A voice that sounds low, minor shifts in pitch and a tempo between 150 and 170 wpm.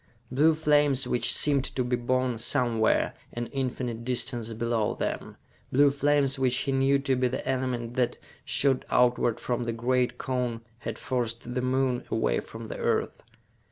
Yes: low, 125 Hz; narrow, 2.0 semitones; average, 160 wpm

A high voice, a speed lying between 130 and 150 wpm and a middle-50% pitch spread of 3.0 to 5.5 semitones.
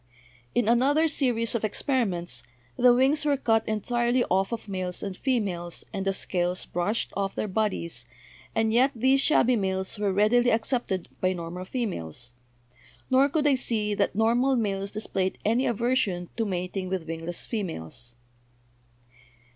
Yes: high, 210 Hz; average, 145 wpm; average, 4.7 semitones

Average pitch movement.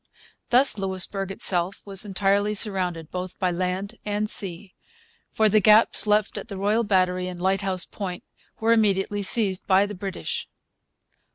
No: narrow, 2.1 semitones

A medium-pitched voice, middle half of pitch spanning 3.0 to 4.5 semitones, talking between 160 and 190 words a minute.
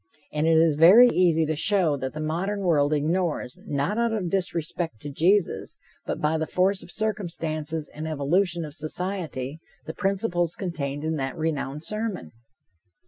Yes: medium, 165 Hz; average, 3.7 semitones; average, 165 wpm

